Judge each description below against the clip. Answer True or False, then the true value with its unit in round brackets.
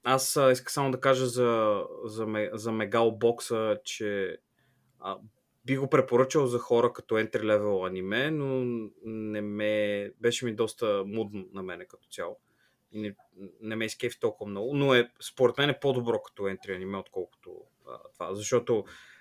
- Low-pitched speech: True (115 Hz)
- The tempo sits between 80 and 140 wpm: False (160 wpm)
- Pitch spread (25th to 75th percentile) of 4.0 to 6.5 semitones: False (3.6 semitones)